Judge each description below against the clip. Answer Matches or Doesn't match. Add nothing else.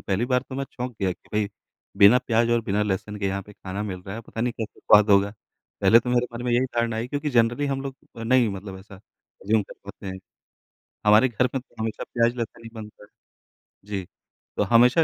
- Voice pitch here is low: Matches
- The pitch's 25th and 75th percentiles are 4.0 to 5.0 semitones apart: Doesn't match